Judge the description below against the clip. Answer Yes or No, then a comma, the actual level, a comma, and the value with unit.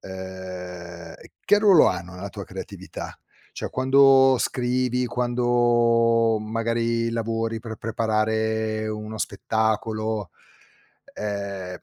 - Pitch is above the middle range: No, low, 110 Hz